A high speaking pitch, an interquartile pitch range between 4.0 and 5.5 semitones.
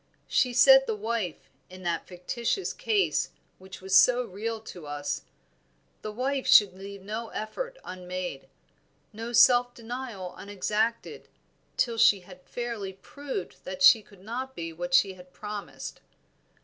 Yes: high, 210 Hz; average, 4.5 semitones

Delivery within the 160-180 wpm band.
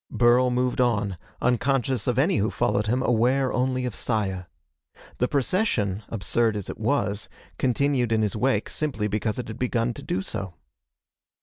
Yes: average, 165 wpm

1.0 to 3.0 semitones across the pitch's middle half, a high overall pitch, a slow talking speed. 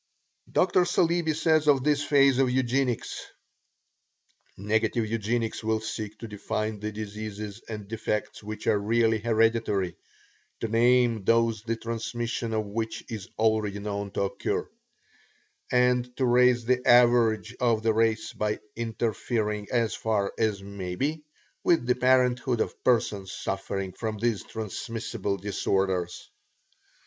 No: narrow, 2.5 semitones; low, 115 Hz; slow, 130 wpm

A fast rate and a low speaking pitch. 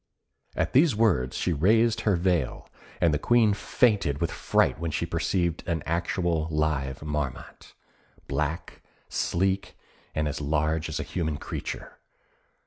No: slow, 135 wpm; very low, 80 Hz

